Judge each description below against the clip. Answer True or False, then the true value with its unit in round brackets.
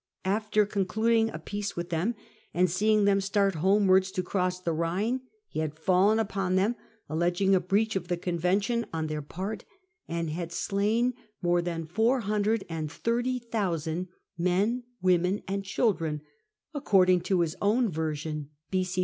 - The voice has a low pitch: False (190 Hz)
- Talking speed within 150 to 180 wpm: False (140 wpm)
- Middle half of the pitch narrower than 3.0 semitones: False (3.6 semitones)